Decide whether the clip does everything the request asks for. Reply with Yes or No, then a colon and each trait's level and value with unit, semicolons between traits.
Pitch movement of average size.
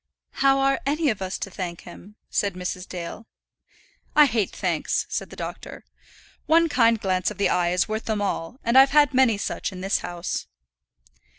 No: wide, 6.5 semitones